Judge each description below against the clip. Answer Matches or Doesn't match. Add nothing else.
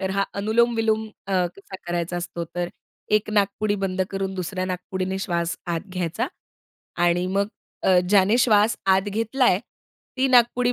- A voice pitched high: Matches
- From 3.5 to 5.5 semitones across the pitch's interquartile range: Doesn't match